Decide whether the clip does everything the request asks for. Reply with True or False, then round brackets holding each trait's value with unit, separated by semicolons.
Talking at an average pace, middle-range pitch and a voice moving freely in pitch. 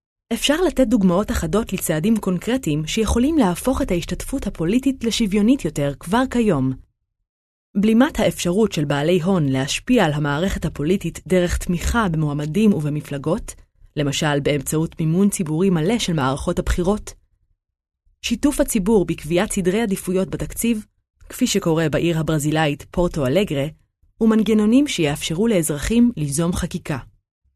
True (115 wpm; 180 Hz; 6.6 semitones)